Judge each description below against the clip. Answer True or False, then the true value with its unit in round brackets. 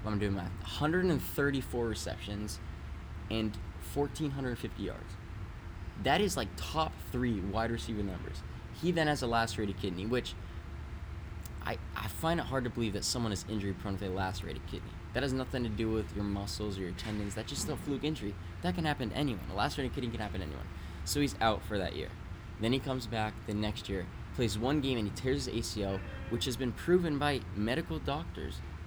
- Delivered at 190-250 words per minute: True (195 wpm)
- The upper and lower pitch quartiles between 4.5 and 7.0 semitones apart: True (5.1 semitones)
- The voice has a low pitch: True (105 Hz)